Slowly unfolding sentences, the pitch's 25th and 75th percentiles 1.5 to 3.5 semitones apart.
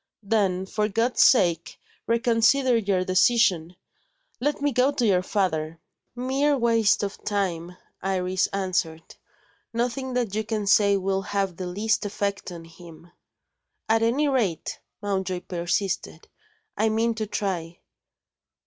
No: slow, 130 wpm; average, 3.9 semitones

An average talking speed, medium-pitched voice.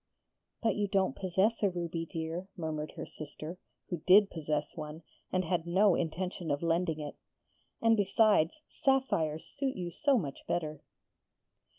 Yes: average, 150 wpm; medium, 175 Hz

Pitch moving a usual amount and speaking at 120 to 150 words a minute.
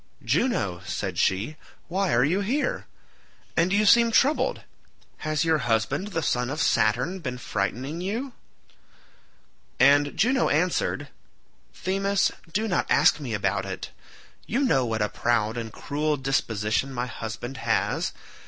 No: wide, 8.7 semitones; slow, 135 wpm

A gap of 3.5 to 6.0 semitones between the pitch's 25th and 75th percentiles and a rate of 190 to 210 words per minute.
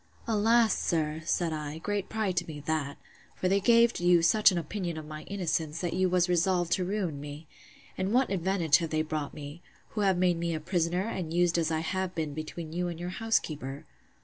No: average, 3.1 semitones; fast, 205 wpm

